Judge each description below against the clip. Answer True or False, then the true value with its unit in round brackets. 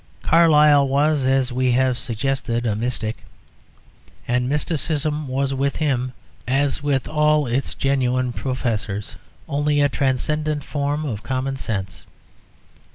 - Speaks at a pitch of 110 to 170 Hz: True (135 Hz)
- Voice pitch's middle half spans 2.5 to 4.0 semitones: True (2.9 semitones)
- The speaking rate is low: True (120 wpm)